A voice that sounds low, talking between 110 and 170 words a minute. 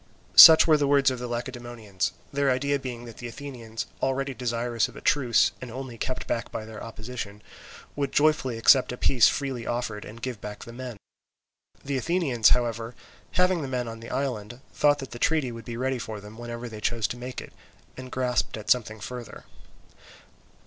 No: low, 120 Hz; average, 190 wpm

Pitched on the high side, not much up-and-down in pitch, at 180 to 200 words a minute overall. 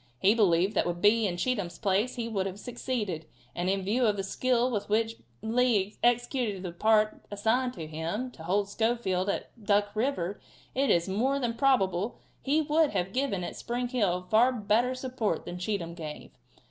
No: high, 210 Hz; average, 4.5 semitones; average, 185 wpm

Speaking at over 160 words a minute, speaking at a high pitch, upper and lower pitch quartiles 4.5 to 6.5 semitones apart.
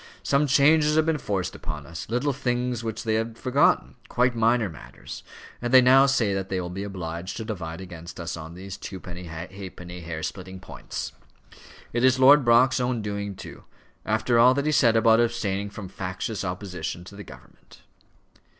No: average, 180 wpm; low, 105 Hz; average, 5.3 semitones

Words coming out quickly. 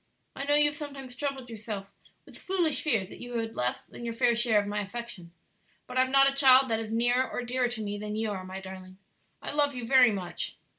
Yes: fast, 245 wpm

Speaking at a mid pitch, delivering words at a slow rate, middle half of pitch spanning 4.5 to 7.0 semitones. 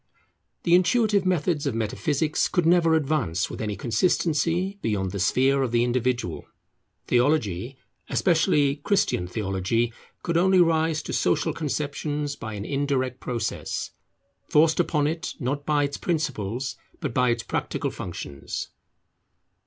Yes: medium, 145 Hz; slow, 130 wpm; wide, 5.6 semitones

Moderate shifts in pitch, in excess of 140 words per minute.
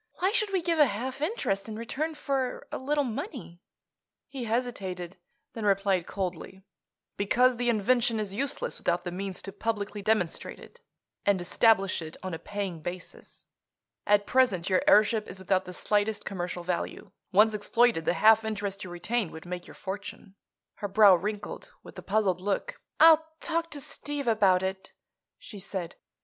Yes: average, 4.5 semitones; average, 165 wpm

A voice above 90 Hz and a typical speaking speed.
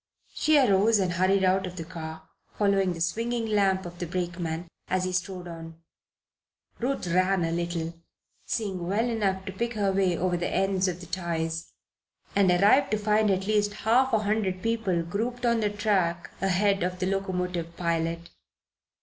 Yes: high, 190 Hz; average, 175 wpm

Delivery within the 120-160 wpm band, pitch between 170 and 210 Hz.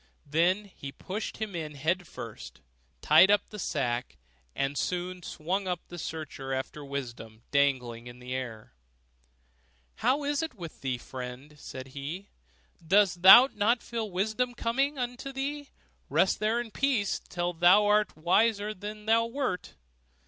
Yes: average, 155 wpm; medium, 185 Hz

